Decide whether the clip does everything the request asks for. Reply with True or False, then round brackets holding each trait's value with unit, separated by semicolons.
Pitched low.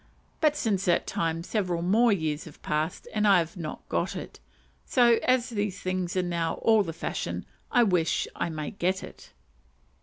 False (185 Hz)